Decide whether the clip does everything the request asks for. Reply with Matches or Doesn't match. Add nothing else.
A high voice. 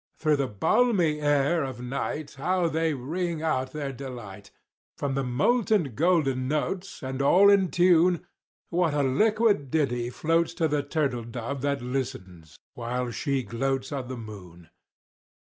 Doesn't match